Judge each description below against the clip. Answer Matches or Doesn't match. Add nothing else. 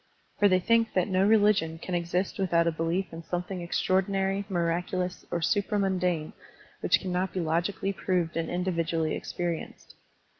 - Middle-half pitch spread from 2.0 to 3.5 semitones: Matches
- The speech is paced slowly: Doesn't match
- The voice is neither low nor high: Matches